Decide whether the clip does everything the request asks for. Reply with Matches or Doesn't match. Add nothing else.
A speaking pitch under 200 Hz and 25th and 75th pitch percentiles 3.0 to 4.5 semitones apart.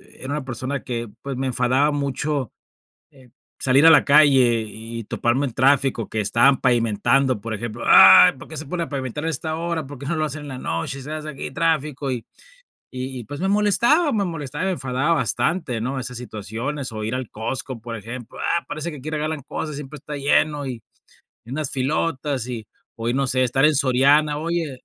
Matches